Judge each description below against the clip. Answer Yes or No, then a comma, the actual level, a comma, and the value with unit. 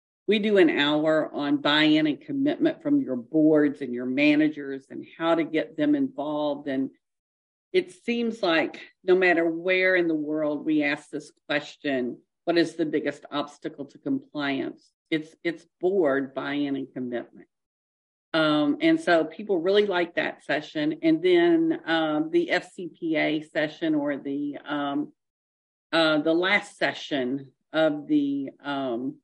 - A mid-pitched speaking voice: Yes, medium, 160 Hz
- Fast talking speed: No, average, 145 wpm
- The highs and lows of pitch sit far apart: Yes, wide, 6.0 semitones